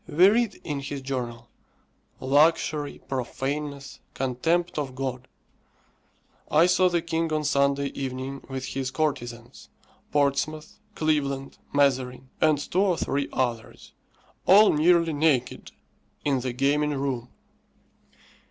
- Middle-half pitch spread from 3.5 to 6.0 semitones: No, average, 2.9 semitones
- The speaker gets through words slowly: Yes, slow, 115 wpm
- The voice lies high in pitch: No, medium, 140 Hz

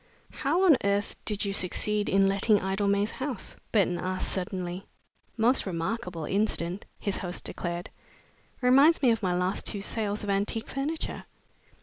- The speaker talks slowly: No, average, 145 wpm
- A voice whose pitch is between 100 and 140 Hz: No, high, 200 Hz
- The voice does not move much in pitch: No, average, 3.4 semitones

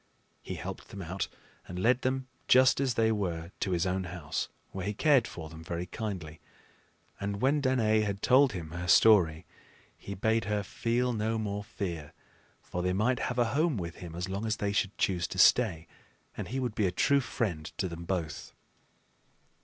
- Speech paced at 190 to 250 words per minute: Yes, average, 195 wpm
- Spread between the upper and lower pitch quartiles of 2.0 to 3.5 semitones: No, average, 4.8 semitones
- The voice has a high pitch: No, low, 100 Hz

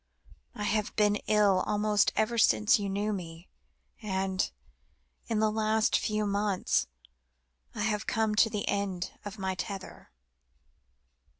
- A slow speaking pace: Yes, slow, 130 wpm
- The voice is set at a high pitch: Yes, high, 210 Hz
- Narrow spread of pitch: Yes, narrow, 1.8 semitones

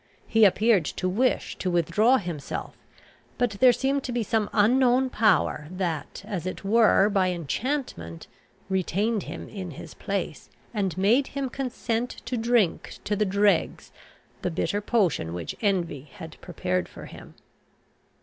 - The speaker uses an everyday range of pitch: Yes, average, 5.0 semitones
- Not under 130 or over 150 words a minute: Yes, average, 145 wpm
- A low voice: No, high, 205 Hz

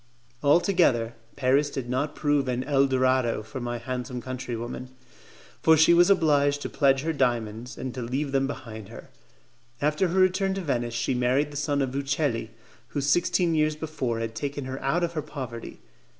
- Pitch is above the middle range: No, low, 135 Hz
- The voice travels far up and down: No, average, 3.4 semitones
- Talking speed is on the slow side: No, average, 180 wpm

